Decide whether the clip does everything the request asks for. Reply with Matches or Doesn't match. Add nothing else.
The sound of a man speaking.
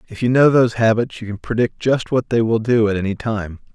Matches